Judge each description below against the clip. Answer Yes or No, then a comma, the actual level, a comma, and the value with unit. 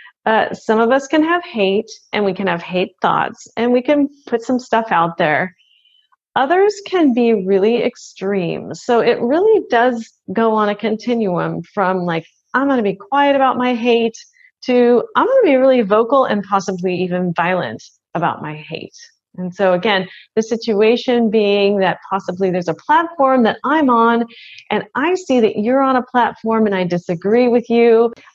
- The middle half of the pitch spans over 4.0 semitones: Yes, average, 4.6 semitones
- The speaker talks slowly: No, average, 175 wpm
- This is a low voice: No, high, 230 Hz